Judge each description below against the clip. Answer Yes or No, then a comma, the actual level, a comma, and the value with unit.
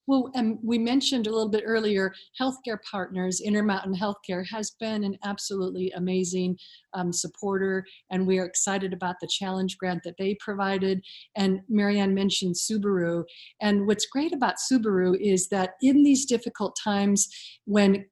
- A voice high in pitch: Yes, high, 195 Hz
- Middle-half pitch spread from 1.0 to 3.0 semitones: Yes, average, 2.7 semitones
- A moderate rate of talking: Yes, average, 150 wpm